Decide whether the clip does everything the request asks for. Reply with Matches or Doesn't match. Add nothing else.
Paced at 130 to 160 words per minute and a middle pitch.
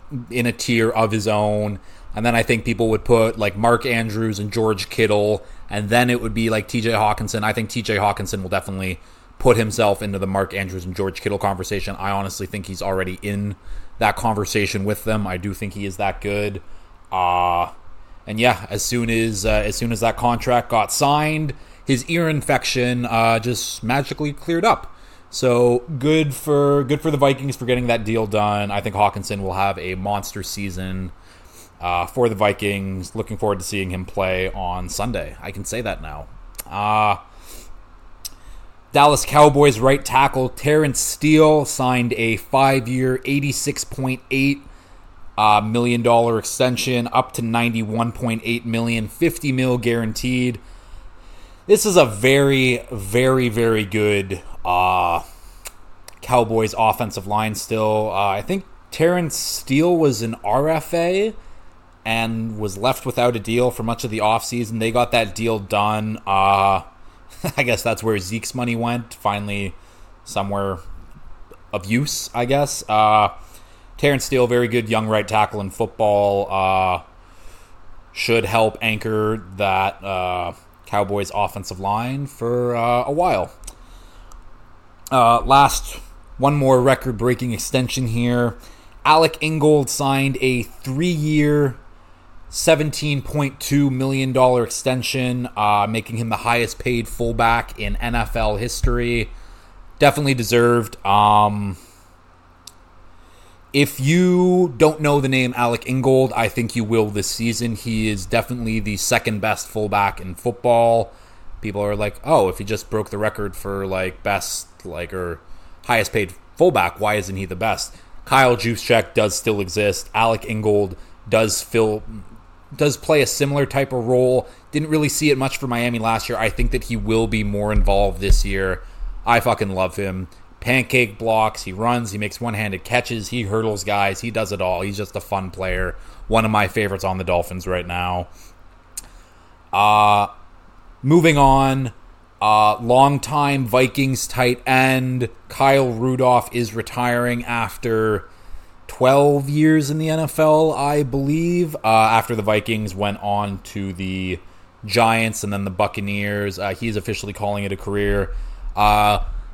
Doesn't match